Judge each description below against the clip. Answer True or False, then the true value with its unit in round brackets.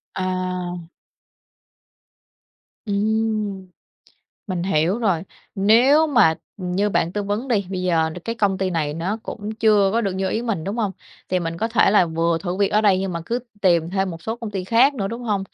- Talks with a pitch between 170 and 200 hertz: True (195 Hz)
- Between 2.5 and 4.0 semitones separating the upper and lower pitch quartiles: True (3.3 semitones)